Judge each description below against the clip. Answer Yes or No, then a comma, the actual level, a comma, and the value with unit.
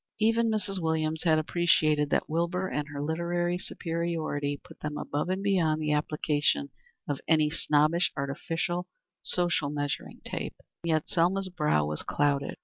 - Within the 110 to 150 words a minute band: Yes, average, 145 wpm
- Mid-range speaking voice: Yes, medium, 160 Hz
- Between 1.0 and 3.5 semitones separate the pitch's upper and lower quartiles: Yes, average, 2.8 semitones